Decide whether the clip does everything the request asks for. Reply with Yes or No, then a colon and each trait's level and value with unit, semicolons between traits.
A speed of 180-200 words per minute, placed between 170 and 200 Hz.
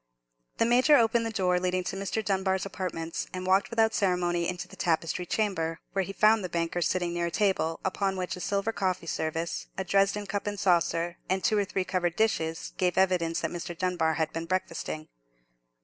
Yes: average, 195 wpm; medium, 185 Hz